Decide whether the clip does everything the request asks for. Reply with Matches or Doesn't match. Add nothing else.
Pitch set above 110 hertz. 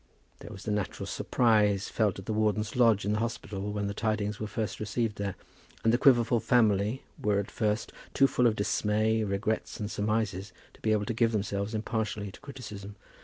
Doesn't match